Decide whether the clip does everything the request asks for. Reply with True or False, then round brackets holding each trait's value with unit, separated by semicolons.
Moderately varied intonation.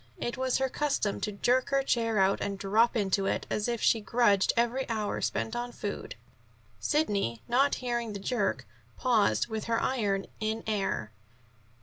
True (3.4 semitones)